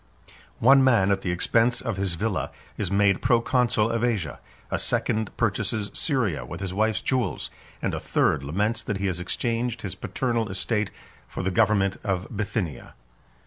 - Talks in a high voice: No, low, 105 Hz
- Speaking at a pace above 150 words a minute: Yes, average, 165 wpm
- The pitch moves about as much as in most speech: Yes, average, 3.4 semitones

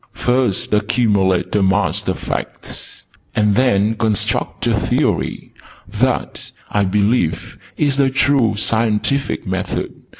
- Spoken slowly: Yes, slow, 110 wpm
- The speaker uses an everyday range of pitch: Yes, average, 3.9 semitones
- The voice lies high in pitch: No, low, 105 Hz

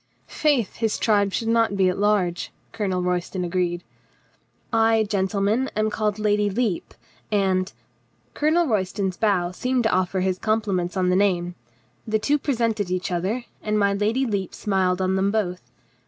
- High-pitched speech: Yes, high, 200 Hz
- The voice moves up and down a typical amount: Yes, average, 3.1 semitones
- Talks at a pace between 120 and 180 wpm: Yes, average, 170 wpm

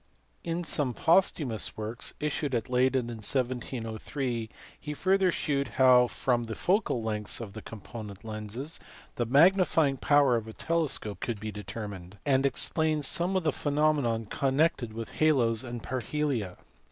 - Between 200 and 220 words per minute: No, average, 145 wpm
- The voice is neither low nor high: No, low, 125 Hz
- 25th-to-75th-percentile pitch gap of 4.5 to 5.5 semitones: Yes, average, 5.0 semitones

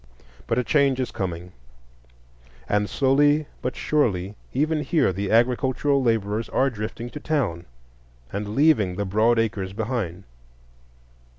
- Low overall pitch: Yes, low, 115 Hz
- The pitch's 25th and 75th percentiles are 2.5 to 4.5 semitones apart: No, average, 5.2 semitones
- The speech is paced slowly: Yes, slow, 125 wpm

